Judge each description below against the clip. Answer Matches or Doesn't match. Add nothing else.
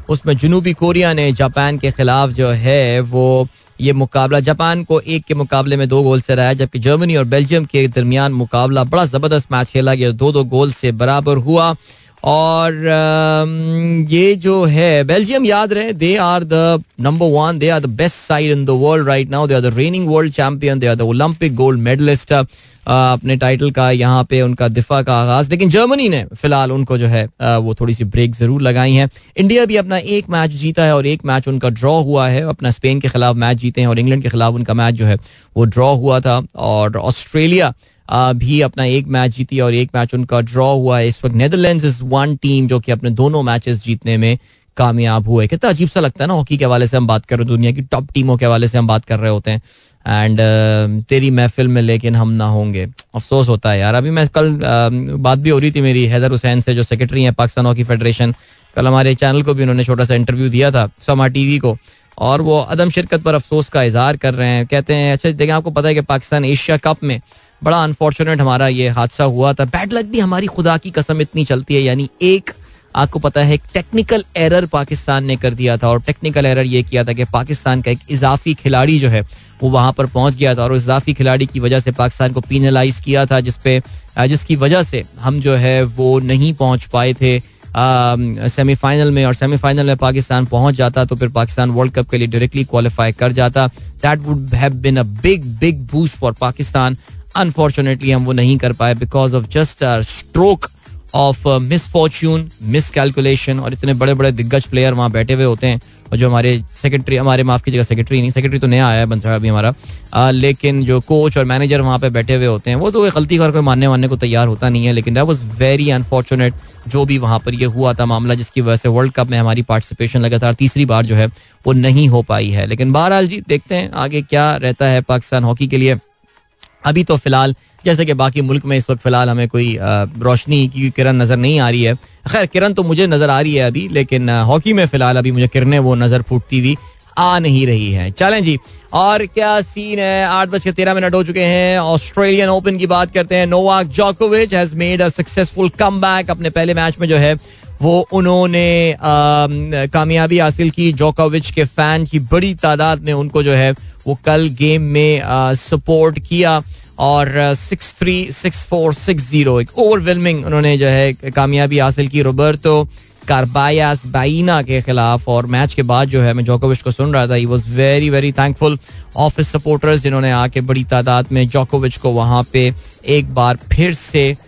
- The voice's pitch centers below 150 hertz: Matches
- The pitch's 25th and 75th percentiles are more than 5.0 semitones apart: Doesn't match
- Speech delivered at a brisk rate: Matches